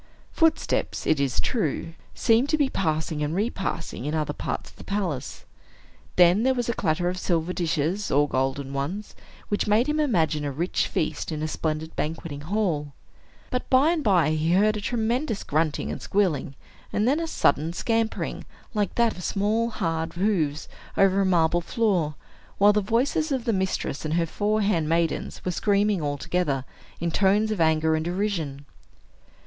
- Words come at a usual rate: Yes, average, 175 wpm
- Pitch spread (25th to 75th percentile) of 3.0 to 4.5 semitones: No, average, 5.3 semitones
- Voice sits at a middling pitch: Yes, medium, 180 Hz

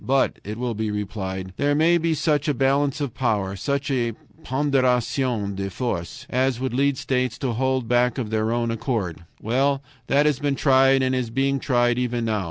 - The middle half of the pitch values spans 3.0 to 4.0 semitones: Yes, average, 3.3 semitones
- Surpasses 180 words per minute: Yes, average, 190 wpm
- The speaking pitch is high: No, low, 125 Hz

